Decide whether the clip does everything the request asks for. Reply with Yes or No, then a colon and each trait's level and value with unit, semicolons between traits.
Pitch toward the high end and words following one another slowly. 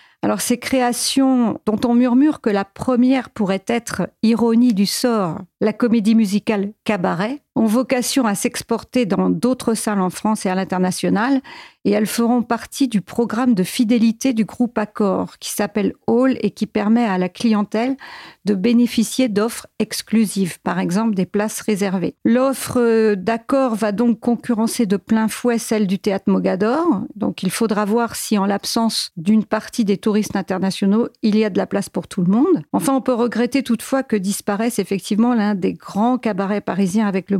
No: high, 220 Hz; average, 175 wpm